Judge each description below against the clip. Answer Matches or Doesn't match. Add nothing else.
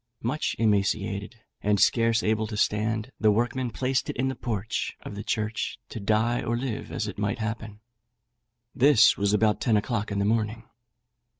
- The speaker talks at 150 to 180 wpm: Matches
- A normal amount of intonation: Doesn't match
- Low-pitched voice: Matches